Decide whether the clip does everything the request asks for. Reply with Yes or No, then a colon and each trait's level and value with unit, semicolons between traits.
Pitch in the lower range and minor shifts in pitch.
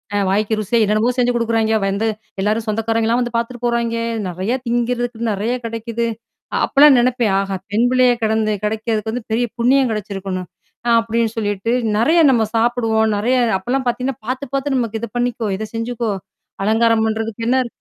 No: high, 230 Hz; narrow, 1.8 semitones